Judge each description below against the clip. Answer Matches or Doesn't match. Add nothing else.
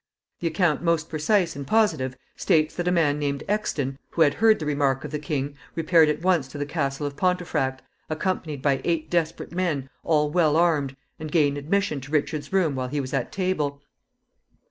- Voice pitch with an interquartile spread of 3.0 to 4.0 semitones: Matches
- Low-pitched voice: Doesn't match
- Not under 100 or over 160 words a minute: Doesn't match